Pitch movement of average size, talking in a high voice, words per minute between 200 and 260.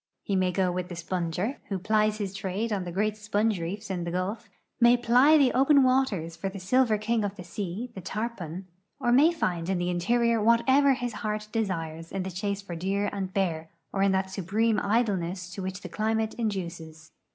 Yes: average, 3.8 semitones; high, 200 Hz; fast, 205 wpm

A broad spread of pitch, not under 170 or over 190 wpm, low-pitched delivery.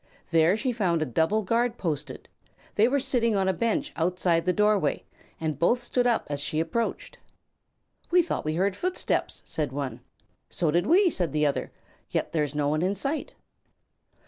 No: wide, 7.0 semitones; average, 180 wpm; medium, 185 Hz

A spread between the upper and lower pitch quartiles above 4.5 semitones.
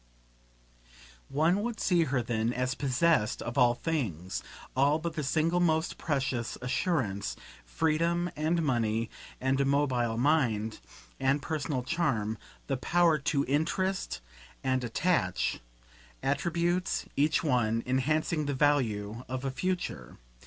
Yes: average, 5.0 semitones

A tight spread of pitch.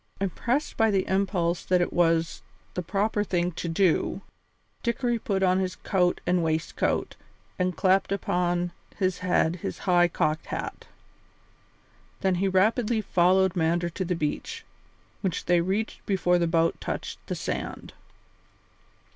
Yes: narrow, 2.2 semitones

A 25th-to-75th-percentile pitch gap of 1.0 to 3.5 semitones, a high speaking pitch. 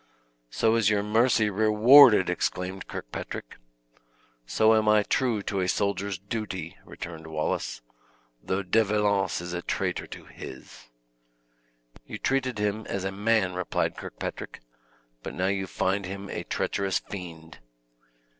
No: average, 2.8 semitones; low, 100 Hz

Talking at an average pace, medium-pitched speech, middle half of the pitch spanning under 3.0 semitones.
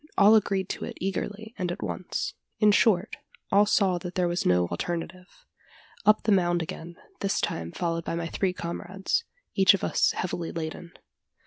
Yes: average, 175 wpm; medium, 180 Hz; narrow, 2.6 semitones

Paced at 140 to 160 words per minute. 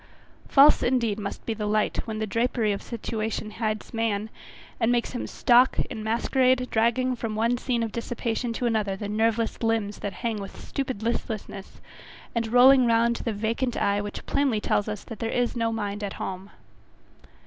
No: average, 180 wpm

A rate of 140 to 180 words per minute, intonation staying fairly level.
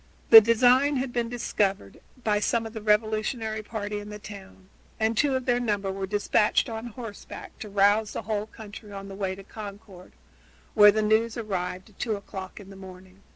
No: average, 195 wpm; narrow, 2.3 semitones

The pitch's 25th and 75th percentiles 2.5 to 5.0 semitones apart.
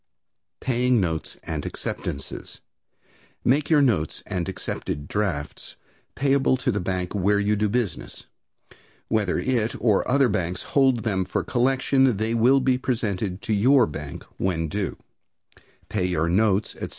No: wide, 5.4 semitones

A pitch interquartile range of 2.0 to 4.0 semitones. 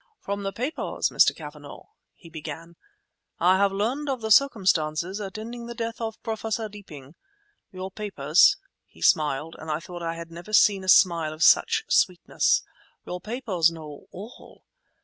No: average, 4.9 semitones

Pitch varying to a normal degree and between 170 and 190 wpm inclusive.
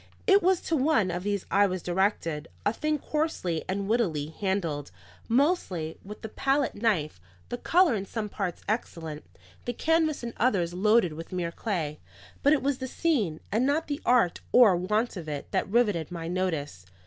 No: wide, 6.8 semitones; average, 180 wpm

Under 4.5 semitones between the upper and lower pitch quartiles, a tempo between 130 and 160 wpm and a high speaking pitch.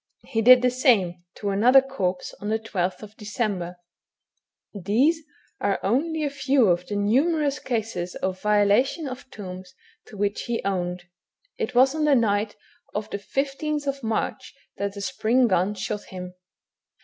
No: average, 5.0 semitones; average, 150 wpm; high, 215 Hz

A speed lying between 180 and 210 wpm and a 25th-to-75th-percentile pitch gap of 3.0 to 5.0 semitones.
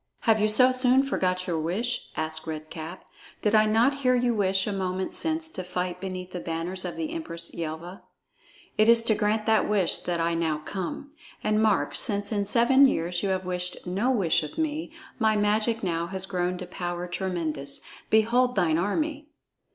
Yes: average, 190 wpm; average, 4.6 semitones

